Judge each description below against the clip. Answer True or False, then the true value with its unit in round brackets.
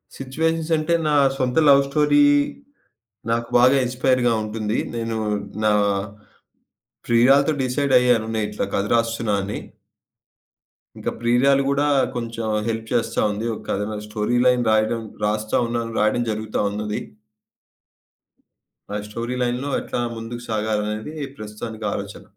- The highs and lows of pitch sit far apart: False (2.9 semitones)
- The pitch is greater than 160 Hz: False (115 Hz)